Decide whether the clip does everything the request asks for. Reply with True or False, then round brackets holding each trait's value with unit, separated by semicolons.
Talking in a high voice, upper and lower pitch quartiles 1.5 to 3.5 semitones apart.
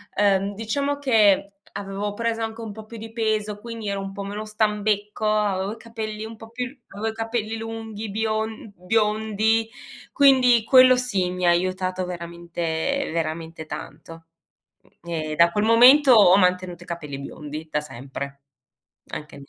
False (210 Hz; 3.9 semitones)